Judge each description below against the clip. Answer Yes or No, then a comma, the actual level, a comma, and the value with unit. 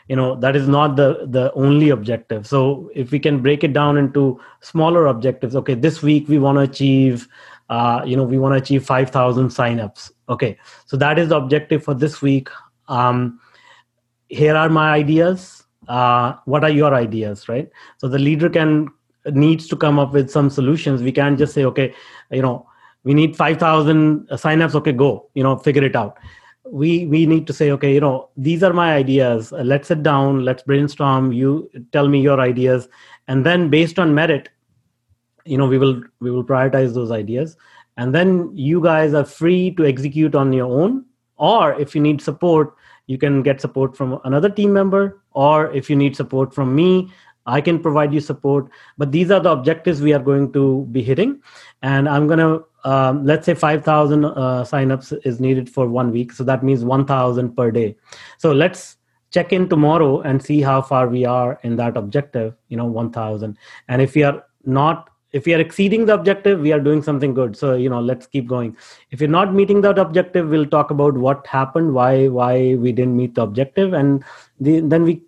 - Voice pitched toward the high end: No, medium, 140 Hz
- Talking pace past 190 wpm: Yes, average, 200 wpm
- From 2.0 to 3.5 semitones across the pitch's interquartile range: Yes, average, 3.1 semitones